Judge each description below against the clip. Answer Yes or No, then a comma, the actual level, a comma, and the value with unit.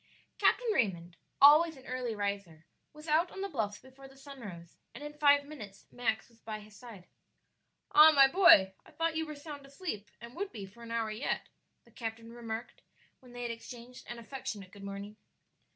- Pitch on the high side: Yes, high, 240 Hz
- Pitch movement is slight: No, average, 5.3 semitones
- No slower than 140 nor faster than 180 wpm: No, average, 195 wpm